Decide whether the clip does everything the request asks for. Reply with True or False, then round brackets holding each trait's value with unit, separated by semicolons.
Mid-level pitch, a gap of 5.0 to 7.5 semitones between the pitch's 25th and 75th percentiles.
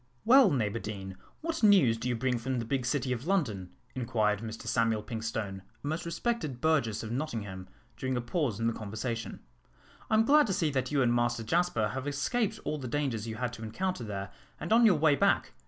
False (125 Hz; 5.6 semitones)